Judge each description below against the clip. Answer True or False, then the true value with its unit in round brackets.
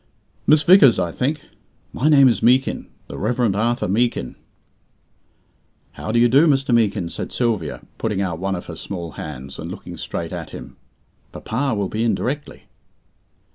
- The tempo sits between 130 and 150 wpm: False (165 wpm)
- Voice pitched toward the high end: False (115 Hz)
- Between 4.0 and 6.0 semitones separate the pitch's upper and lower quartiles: True (5.6 semitones)